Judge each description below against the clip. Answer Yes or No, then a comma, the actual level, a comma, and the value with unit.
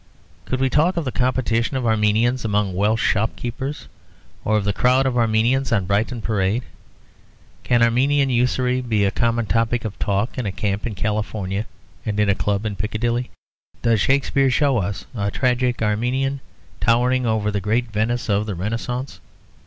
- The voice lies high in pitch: No, low, 115 Hz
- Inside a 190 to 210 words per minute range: No, average, 170 wpm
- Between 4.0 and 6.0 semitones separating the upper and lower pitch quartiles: No, average, 3.2 semitones